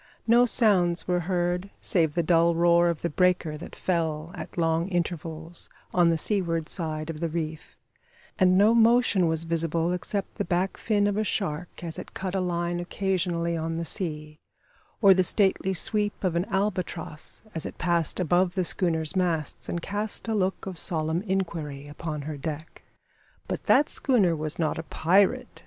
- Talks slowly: No, average, 180 wpm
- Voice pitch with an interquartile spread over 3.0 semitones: No, average, 2.7 semitones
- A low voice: No, medium, 175 Hz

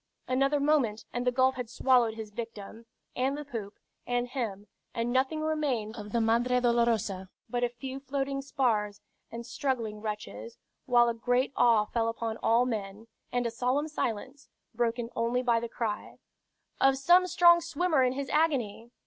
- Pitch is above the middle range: Yes, high, 245 Hz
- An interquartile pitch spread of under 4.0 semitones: Yes, average, 3.0 semitones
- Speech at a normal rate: Yes, average, 165 wpm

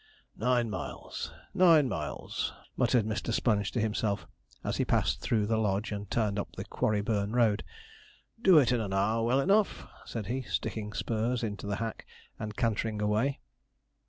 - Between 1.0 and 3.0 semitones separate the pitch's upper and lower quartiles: Yes, average, 2.7 semitones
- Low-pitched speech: Yes, low, 110 Hz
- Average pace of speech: Yes, average, 160 wpm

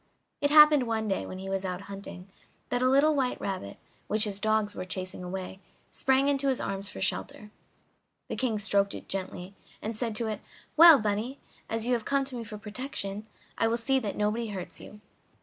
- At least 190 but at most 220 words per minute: Yes, average, 200 wpm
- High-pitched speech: Yes, high, 215 Hz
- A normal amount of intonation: Yes, average, 4.4 semitones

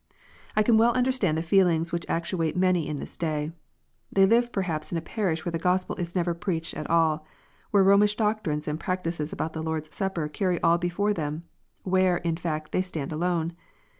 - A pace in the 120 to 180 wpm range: No, average, 195 wpm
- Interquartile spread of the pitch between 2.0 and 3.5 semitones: Yes, average, 3.1 semitones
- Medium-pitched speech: Yes, medium, 170 Hz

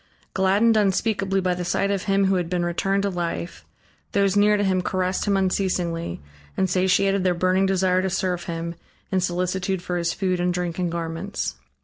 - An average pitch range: No, narrow, 1.7 semitones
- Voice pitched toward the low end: No, medium, 185 Hz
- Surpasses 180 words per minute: Yes, average, 190 wpm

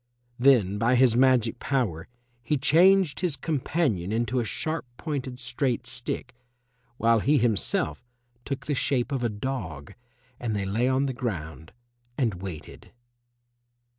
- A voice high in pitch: No, low, 125 Hz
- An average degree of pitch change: Yes, average, 4.5 semitones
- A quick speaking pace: No, slow, 135 wpm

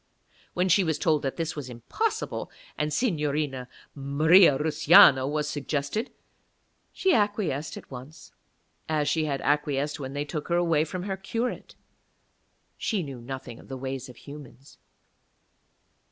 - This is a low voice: No, medium, 150 Hz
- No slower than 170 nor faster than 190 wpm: No, average, 140 wpm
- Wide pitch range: No, average, 3.7 semitones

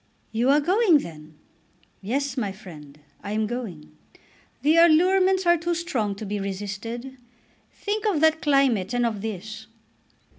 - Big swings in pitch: Yes, wide, 7.9 semitones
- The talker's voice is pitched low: No, high, 240 Hz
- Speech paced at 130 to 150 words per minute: Yes, average, 145 wpm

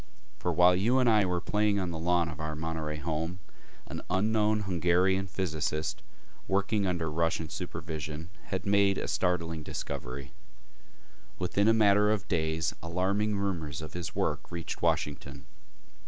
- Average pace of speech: Yes, average, 145 wpm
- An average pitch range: Yes, average, 3.9 semitones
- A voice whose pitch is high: No, very low, 90 Hz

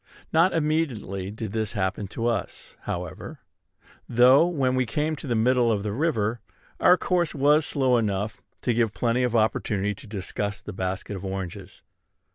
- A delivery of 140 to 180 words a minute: Yes, average, 165 wpm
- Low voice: Yes, low, 115 Hz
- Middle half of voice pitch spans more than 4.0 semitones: Yes, average, 4.7 semitones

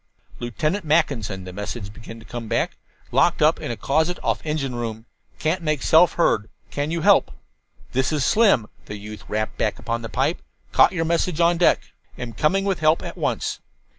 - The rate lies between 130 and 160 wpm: No, average, 180 wpm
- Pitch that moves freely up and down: Yes, wide, 6.8 semitones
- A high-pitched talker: No, medium, 140 Hz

